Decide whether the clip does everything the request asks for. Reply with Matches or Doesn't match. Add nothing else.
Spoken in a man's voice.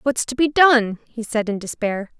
Doesn't match